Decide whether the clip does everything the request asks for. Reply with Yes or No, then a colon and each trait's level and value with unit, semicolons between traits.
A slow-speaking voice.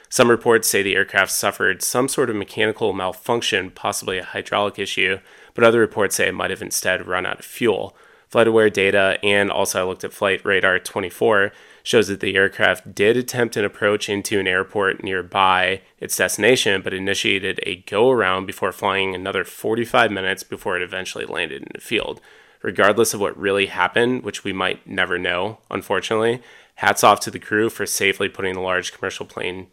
No: average, 180 wpm